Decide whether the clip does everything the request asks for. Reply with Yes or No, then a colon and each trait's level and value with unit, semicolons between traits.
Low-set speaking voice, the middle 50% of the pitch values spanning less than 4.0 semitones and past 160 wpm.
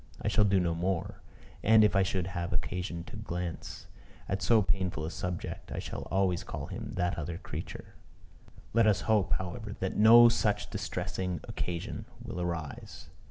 Yes: very low, 95 Hz; average, 2.9 semitones; average, 170 wpm